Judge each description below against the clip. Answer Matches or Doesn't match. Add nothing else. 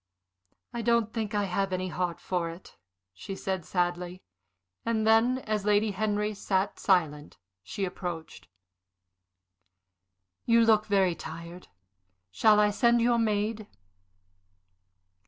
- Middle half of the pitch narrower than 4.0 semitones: Matches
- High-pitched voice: Matches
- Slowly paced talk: Matches